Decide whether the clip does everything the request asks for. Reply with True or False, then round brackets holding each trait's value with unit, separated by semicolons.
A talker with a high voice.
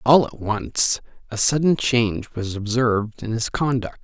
False (115 Hz)